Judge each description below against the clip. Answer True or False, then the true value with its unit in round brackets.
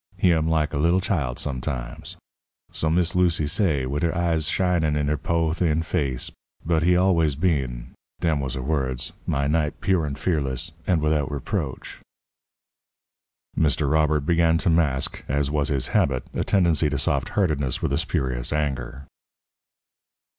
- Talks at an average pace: True (160 wpm)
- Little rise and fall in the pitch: False (3.2 semitones)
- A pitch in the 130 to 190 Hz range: False (75 Hz)